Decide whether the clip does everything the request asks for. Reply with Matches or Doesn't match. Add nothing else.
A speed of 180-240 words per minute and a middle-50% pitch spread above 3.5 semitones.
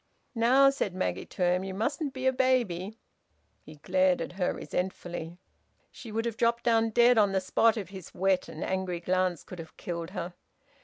Matches